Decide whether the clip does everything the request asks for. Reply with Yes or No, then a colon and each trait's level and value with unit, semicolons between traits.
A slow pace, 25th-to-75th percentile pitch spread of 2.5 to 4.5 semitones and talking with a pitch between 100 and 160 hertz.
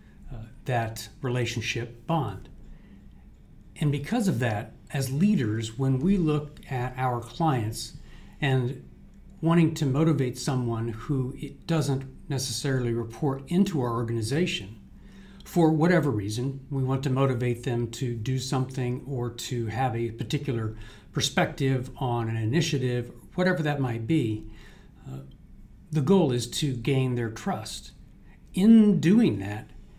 Yes: slow, 130 wpm; average, 4.2 semitones; low, 130 Hz